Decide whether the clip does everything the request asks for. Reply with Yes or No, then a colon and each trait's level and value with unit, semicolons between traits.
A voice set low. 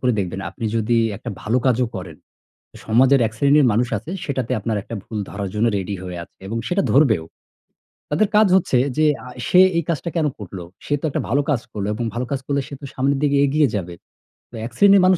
Yes: low, 125 Hz